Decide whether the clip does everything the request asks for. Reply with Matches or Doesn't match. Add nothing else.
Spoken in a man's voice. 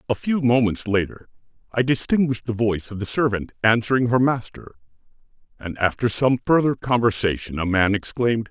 Matches